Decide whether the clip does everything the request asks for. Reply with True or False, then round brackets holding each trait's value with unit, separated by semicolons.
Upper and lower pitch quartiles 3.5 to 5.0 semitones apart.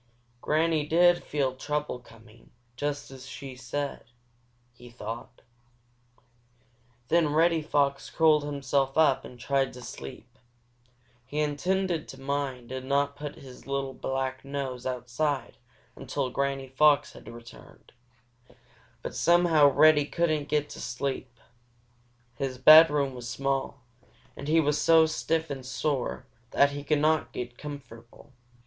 False (2.6 semitones)